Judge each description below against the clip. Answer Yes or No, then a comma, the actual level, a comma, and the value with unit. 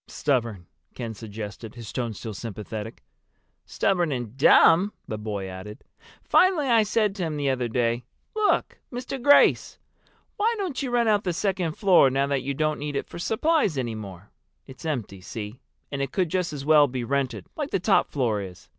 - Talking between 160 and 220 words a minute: Yes, average, 185 wpm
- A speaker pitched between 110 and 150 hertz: Yes, medium, 140 Hz